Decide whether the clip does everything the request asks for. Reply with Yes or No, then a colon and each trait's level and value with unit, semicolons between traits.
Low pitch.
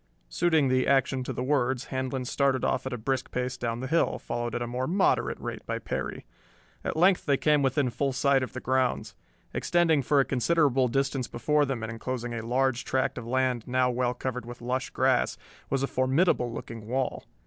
Yes: low, 130 Hz